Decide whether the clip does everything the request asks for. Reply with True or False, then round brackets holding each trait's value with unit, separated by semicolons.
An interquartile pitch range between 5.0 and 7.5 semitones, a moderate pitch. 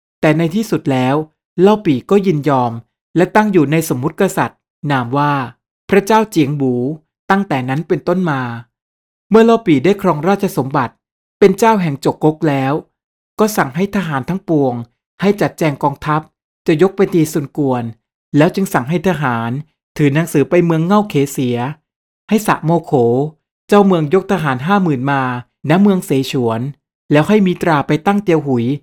True (5.4 semitones; 155 Hz)